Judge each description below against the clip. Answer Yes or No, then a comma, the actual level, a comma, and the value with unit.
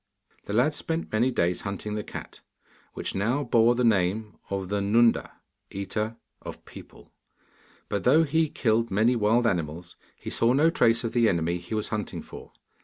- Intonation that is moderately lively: Yes, average, 3.4 semitones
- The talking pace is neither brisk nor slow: Yes, average, 175 wpm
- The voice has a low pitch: Yes, low, 110 Hz